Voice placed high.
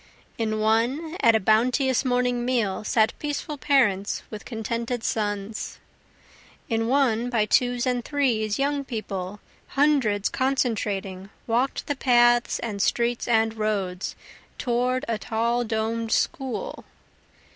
Yes: high, 235 Hz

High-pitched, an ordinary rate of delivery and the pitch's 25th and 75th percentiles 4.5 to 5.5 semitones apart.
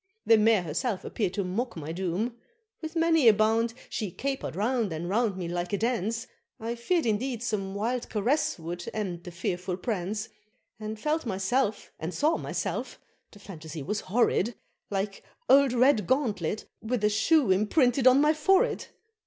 Yes: high, 215 Hz; average, 160 wpm; average, 4.9 semitones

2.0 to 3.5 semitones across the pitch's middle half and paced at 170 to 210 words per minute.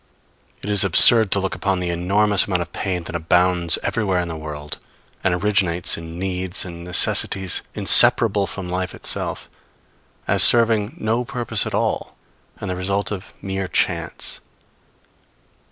No: narrow, 2.6 semitones; average, 150 wpm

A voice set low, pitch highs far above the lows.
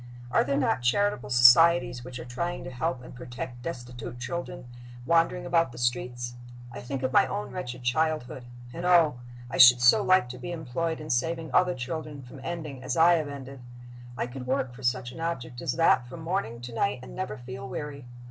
No: low, 130 Hz; average, 5.0 semitones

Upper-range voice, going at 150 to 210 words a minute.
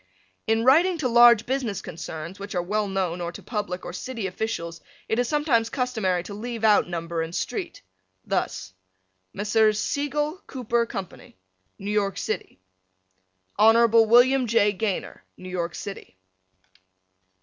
No: high, 215 Hz; average, 140 wpm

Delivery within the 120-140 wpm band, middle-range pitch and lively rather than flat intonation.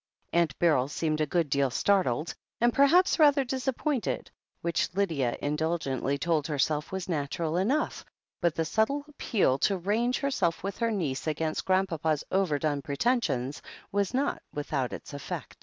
No: average, 155 wpm; medium, 170 Hz; wide, 6.9 semitones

